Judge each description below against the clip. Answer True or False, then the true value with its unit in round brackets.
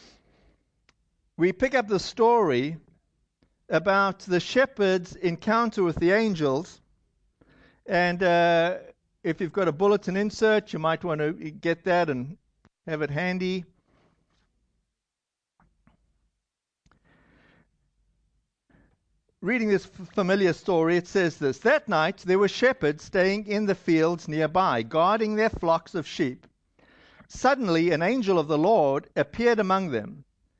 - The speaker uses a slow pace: True (120 wpm)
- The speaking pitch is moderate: True (180 Hz)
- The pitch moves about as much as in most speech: True (3.6 semitones)